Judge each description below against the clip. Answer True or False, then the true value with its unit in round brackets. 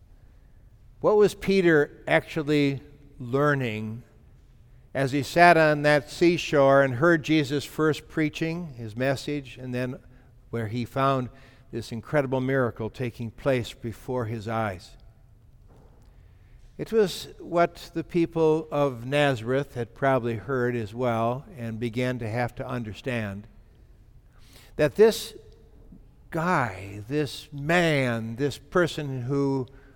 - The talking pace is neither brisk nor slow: False (115 wpm)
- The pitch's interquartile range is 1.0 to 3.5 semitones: False (4.3 semitones)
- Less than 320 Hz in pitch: True (135 Hz)